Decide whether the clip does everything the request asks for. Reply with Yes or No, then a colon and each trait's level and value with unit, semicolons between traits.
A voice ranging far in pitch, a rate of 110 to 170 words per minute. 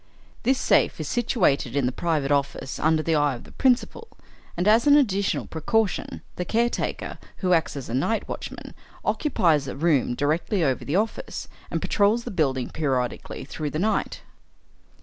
Yes: wide, 7.4 semitones; average, 165 wpm